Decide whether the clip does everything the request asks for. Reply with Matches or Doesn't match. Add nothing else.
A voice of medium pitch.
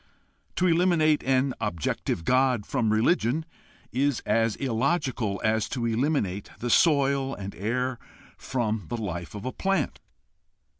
Doesn't match